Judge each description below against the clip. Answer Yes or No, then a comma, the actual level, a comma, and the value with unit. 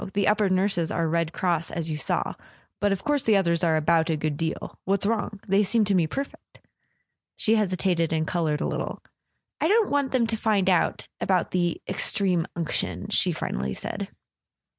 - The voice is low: No, medium, 185 Hz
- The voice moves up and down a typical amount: Yes, average, 4.0 semitones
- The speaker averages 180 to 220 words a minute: Yes, average, 185 wpm